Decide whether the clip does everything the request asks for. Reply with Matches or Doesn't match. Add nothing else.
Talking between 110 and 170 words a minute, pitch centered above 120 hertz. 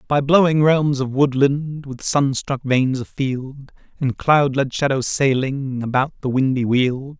Matches